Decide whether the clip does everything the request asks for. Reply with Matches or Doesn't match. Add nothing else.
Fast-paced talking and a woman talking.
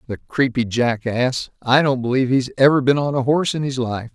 Doesn't match